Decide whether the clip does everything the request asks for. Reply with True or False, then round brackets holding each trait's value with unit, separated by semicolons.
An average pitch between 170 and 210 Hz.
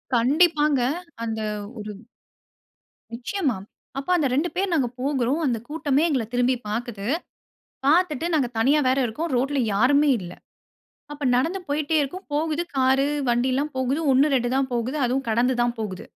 False (270 Hz)